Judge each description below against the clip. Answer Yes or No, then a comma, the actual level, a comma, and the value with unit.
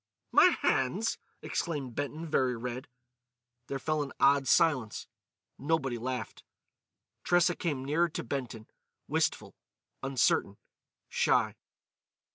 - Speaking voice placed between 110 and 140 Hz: Yes, low, 135 Hz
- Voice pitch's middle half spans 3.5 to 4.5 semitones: Yes, average, 3.8 semitones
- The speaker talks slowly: Yes, slow, 100 wpm